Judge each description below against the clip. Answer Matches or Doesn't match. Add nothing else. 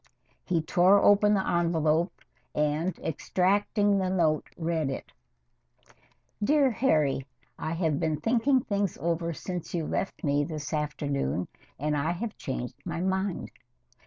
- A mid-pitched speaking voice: Matches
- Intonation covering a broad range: Doesn't match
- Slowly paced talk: Matches